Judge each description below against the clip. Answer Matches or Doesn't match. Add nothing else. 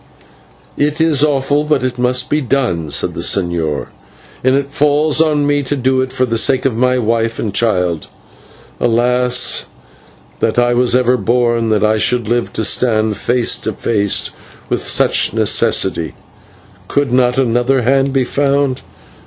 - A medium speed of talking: Matches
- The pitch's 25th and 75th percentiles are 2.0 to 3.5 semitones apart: Matches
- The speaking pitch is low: Matches